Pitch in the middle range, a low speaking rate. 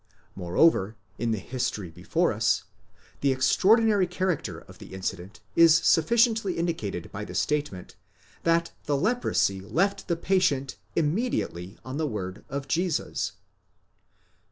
Yes: medium, 150 Hz; slow, 125 wpm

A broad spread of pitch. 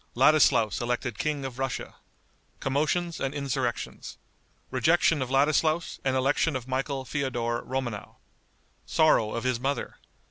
No: average, 2.9 semitones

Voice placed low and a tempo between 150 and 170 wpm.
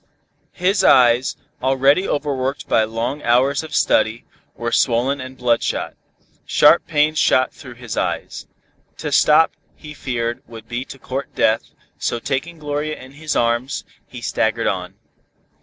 No: low, 130 Hz; average, 140 wpm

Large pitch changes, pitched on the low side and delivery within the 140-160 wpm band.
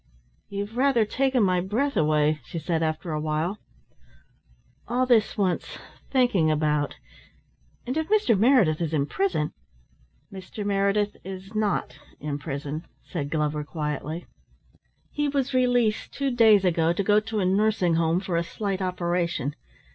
No: wide, 5.9 semitones; medium, 185 Hz; average, 145 wpm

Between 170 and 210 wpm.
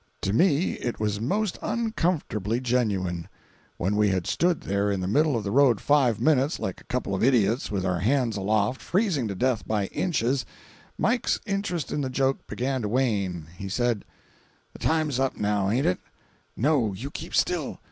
Yes: average, 180 wpm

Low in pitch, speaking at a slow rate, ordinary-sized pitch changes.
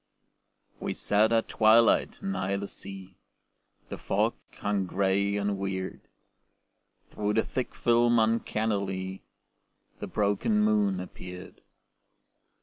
Yes: low, 105 Hz; slow, 105 wpm; average, 3.0 semitones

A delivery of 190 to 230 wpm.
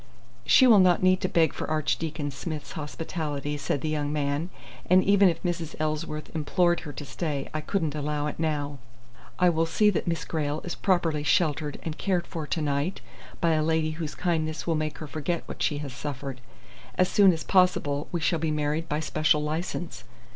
Yes: average, 195 wpm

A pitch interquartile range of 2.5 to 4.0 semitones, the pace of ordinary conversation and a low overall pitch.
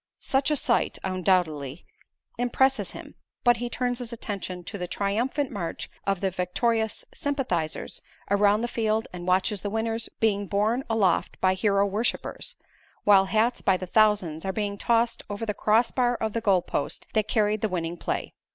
No: average, 3.5 semitones; average, 170 wpm; high, 210 Hz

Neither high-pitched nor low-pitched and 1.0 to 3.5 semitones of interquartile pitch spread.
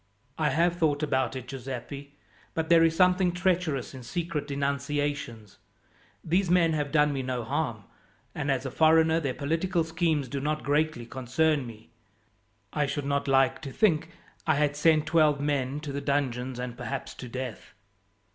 Yes: medium, 145 Hz; average, 3.2 semitones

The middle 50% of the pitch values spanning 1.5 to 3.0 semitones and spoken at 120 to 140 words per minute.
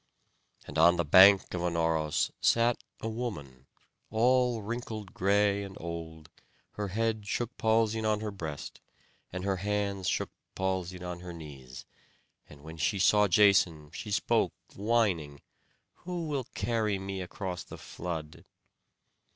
No: average, 4.6 semitones; slow, 135 wpm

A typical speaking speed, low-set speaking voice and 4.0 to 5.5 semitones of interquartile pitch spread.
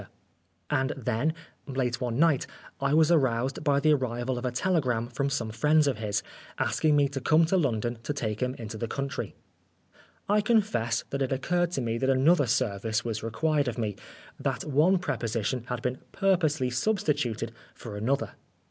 Yes: average, 180 wpm; low, 130 Hz; average, 4.4 semitones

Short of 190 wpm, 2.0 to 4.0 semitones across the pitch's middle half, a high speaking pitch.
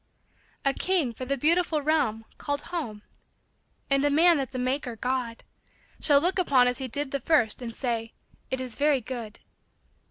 Yes: average, 180 wpm; average, 3.5 semitones; very high, 270 Hz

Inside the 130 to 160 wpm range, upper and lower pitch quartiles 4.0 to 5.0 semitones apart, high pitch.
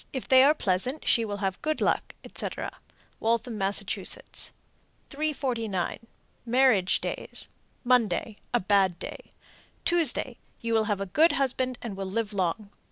Yes: average, 140 wpm; average, 4.7 semitones; high, 225 Hz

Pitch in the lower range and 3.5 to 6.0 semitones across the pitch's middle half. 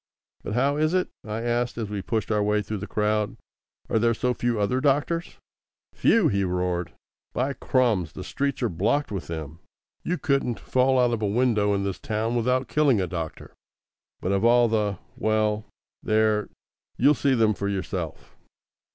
Yes: low, 110 Hz; average, 3.8 semitones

